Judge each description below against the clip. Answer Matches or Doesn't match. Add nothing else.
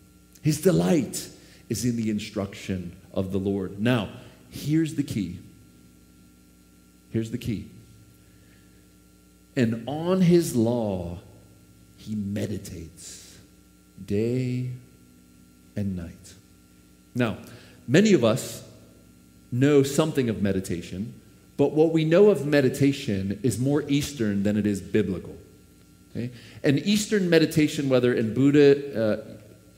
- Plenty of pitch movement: Matches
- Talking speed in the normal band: Doesn't match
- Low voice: Matches